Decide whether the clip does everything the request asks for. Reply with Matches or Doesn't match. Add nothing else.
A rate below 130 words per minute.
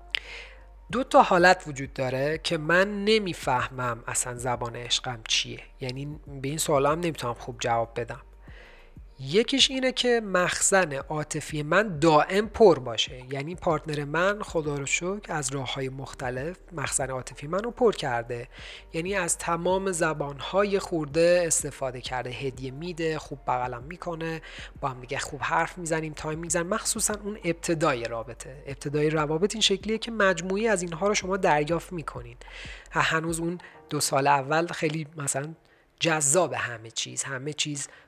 Doesn't match